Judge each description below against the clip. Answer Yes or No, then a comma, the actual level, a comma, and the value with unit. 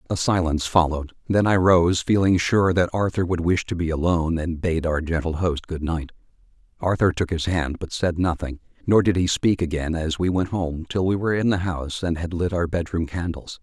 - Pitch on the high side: No, very low, 85 Hz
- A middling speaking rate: No, fast, 225 wpm